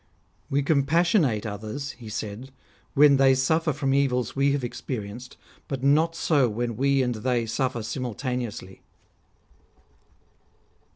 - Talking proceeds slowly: Yes, slow, 130 wpm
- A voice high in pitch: No, low, 130 Hz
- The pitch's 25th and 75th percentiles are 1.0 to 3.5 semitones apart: Yes, average, 3.1 semitones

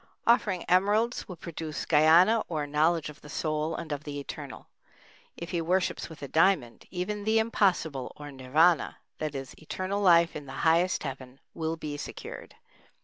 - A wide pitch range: No, average, 3.7 semitones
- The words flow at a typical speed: Yes, average, 165 wpm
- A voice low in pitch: No, medium, 160 Hz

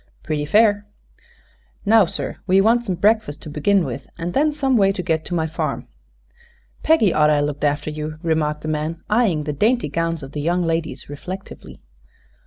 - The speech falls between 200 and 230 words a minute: No, average, 185 wpm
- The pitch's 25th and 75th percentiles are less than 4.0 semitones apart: No, average, 5.2 semitones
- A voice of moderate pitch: Yes, medium, 165 Hz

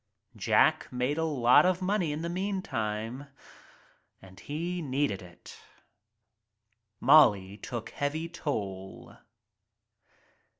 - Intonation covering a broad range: Yes, wide, 7.7 semitones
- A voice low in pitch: No, medium, 145 Hz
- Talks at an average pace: No, slow, 95 wpm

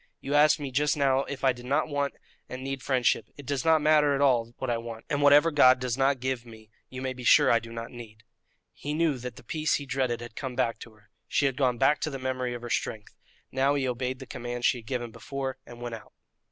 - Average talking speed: No, fast, 260 wpm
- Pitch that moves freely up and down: No, average, 2.8 semitones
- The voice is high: No, low, 130 Hz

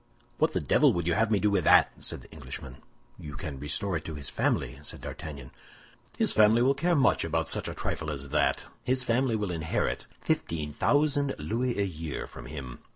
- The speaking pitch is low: Yes, very low, 85 Hz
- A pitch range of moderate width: No, wide, 7.7 semitones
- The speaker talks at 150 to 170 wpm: No, fast, 205 wpm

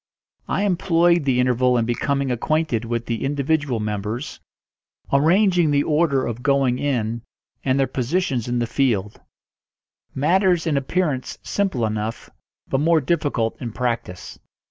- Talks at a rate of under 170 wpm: Yes, slow, 135 wpm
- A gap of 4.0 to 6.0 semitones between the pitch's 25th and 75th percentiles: Yes, average, 4.9 semitones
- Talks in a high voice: No, low, 135 Hz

